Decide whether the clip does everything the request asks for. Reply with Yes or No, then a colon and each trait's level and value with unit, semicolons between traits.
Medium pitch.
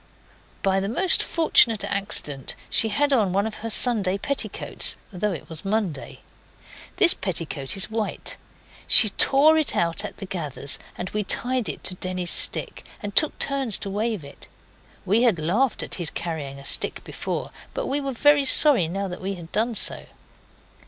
No: high, 205 Hz